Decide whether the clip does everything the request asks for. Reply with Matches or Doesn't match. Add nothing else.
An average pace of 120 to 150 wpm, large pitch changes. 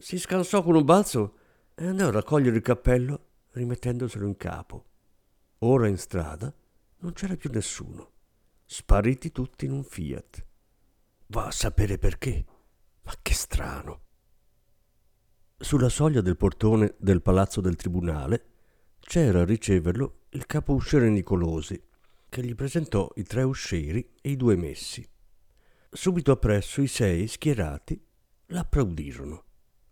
Matches